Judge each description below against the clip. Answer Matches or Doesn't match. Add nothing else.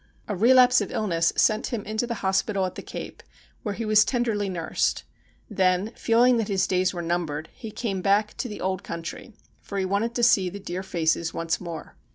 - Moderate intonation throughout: Matches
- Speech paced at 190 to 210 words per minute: Matches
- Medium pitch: Doesn't match